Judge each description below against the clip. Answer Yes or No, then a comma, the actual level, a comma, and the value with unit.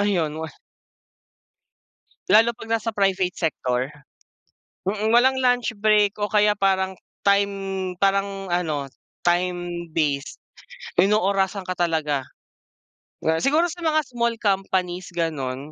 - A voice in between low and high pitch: No, high, 195 Hz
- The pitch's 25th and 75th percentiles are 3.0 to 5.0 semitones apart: Yes, average, 3.3 semitones